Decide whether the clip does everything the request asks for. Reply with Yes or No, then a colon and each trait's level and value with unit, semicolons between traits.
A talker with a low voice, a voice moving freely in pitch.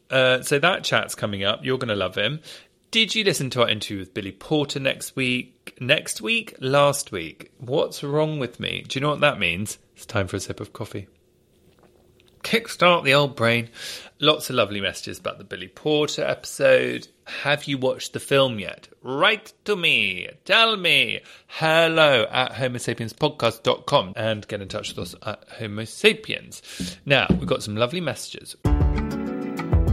Yes: low, 130 Hz; wide, 5.9 semitones